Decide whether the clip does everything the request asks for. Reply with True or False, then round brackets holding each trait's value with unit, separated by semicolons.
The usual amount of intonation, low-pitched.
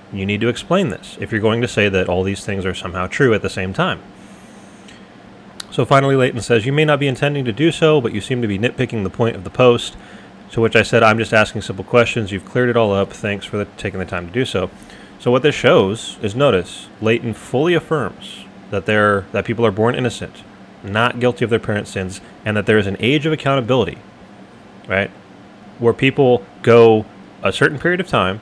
True (3.9 semitones; 115 Hz)